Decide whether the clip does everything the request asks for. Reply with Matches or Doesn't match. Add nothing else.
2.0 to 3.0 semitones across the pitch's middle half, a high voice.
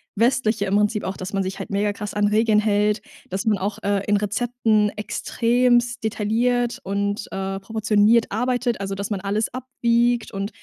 Matches